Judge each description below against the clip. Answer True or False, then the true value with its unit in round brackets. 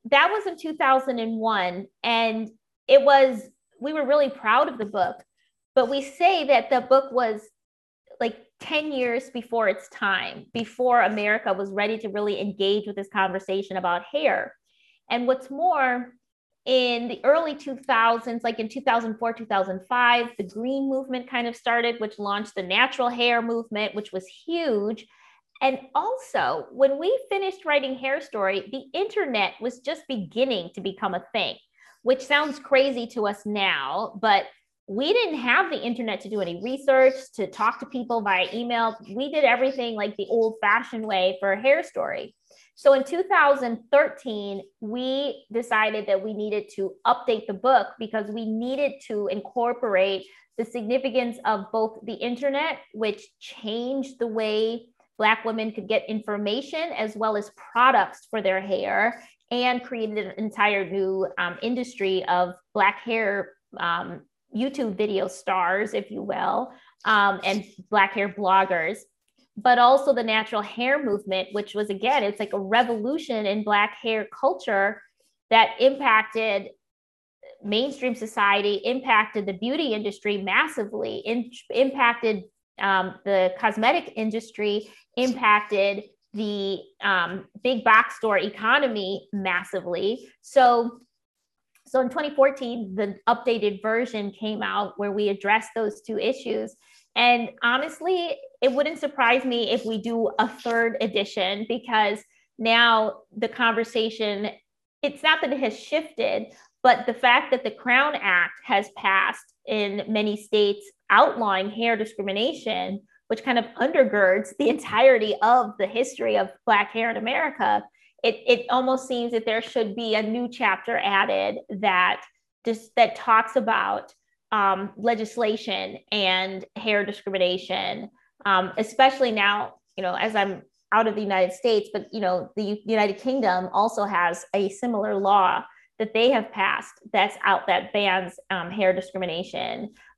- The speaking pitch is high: True (225 Hz)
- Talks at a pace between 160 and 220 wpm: False (145 wpm)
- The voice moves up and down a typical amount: True (3.9 semitones)